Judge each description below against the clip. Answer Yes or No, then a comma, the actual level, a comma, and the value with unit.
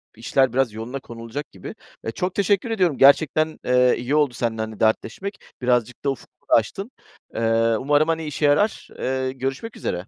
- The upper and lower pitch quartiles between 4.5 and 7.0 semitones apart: Yes, average, 5.2 semitones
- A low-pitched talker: Yes, low, 130 Hz